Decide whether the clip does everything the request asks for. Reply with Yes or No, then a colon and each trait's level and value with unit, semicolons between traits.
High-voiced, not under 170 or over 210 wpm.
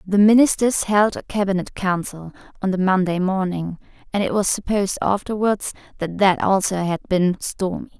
No: high, 195 Hz; average, 160 wpm